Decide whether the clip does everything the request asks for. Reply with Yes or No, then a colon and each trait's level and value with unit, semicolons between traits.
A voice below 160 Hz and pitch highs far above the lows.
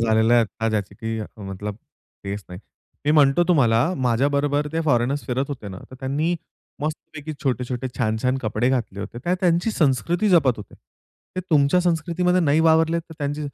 Yes: medium, 140 Hz; wide, 5.9 semitones